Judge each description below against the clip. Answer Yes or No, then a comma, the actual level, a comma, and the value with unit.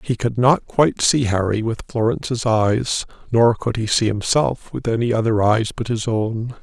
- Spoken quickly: No, average, 190 wpm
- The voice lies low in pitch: Yes, low, 115 Hz